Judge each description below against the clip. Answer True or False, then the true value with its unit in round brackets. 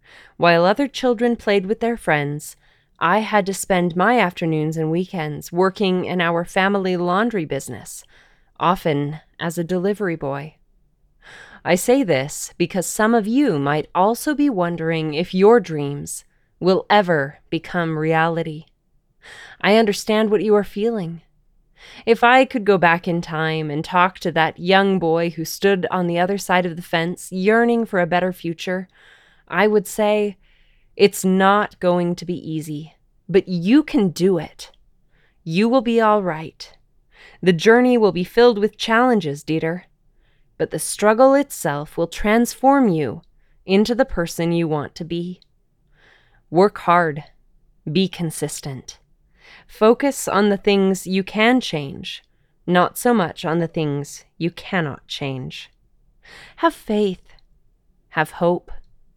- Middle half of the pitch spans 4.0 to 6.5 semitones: True (4.5 semitones)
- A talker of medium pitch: True (180 Hz)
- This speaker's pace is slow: False (145 wpm)